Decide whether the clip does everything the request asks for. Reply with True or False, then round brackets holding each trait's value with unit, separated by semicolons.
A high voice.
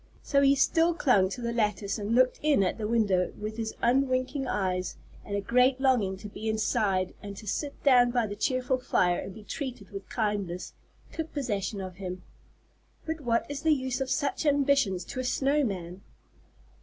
True (235 Hz)